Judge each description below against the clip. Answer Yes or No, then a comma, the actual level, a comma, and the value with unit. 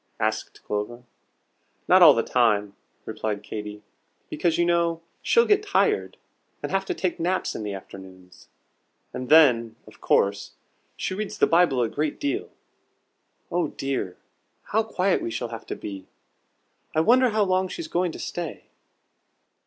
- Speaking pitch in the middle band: Yes, medium, 155 Hz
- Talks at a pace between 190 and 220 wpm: No, average, 155 wpm